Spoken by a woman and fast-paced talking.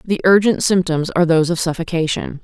No: female; average, 170 wpm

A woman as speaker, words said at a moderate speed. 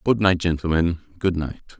No: male; average, 165 wpm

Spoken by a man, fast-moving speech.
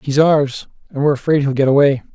Yes: male; fast, 250 wpm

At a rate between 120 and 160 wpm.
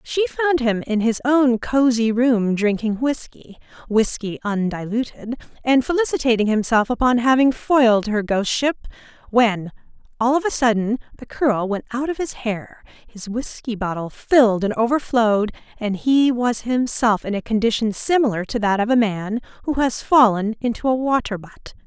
Yes: average, 155 wpm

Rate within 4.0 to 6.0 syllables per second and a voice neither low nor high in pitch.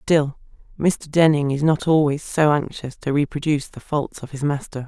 Yes: 4.9 syllables/s; medium, 145 Hz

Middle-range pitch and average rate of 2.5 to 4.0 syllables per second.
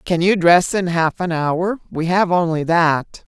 Yes: medium, 175 Hz; 3.9 syllables/s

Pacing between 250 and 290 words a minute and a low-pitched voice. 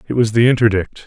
No: fast, 225 wpm; low, 110 Hz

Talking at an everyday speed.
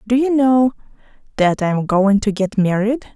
Yes: average, 190 wpm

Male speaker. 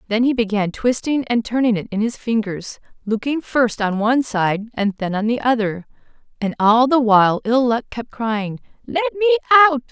No: female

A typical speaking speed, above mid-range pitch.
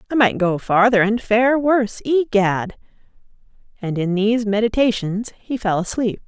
Yes: average, 145 wpm; high, 220 Hz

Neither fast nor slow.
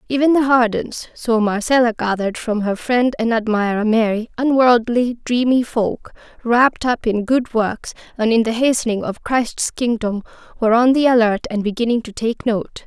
Yes: average, 160 wpm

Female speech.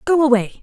Yes: female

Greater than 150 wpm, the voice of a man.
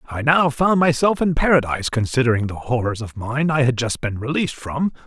Yes: average, 200 wpm; male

